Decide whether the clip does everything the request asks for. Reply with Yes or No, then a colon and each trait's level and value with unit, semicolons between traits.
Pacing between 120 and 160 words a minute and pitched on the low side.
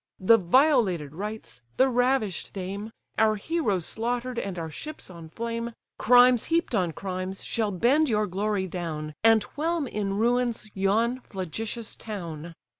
No: average, 140 wpm; high, 215 Hz